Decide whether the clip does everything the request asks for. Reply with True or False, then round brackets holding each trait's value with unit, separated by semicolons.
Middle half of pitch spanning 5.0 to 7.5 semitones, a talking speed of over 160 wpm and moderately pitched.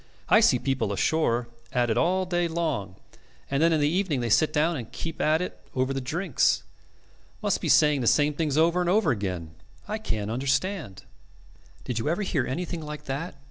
True (5.5 semitones; 195 wpm; 150 Hz)